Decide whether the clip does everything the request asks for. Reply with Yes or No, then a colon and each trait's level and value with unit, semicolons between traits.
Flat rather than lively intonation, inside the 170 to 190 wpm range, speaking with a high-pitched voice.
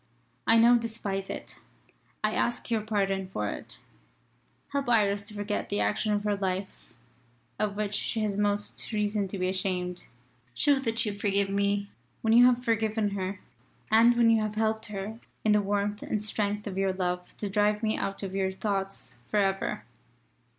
Yes: narrow, 1.9 semitones; average, 180 wpm; high, 205 Hz